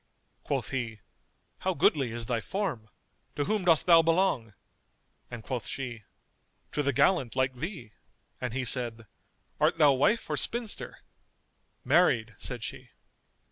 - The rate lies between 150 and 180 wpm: No, average, 140 wpm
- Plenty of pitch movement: Yes, wide, 6.1 semitones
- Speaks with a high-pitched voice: No, low, 130 Hz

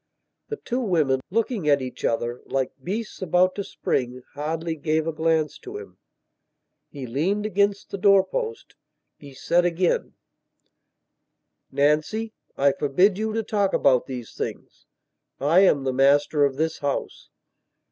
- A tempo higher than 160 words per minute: No, average, 145 wpm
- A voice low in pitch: No, medium, 160 Hz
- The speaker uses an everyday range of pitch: No, wide, 6.2 semitones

